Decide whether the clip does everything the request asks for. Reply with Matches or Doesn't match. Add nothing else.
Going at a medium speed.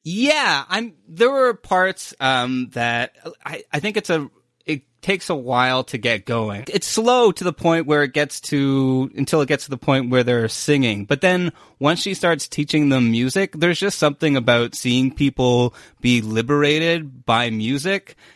Matches